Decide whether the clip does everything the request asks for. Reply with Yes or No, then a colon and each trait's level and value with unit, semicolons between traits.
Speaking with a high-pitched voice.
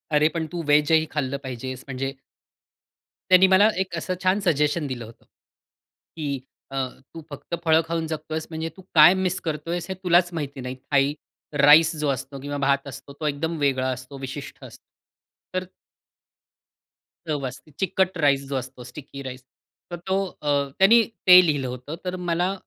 No: medium, 150 Hz